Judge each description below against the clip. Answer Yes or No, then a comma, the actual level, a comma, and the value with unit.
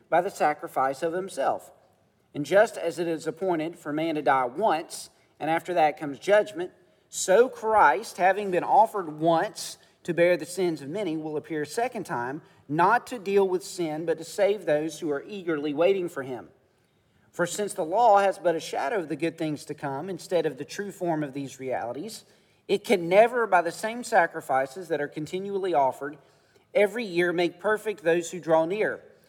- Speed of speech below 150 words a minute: No, average, 195 wpm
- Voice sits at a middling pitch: Yes, medium, 170 Hz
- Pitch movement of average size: Yes, average, 4.2 semitones